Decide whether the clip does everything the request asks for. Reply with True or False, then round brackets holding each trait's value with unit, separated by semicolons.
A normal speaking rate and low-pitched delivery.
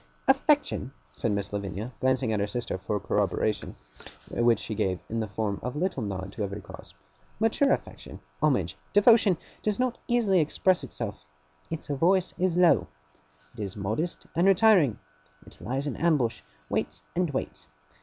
True (160 wpm; 130 Hz)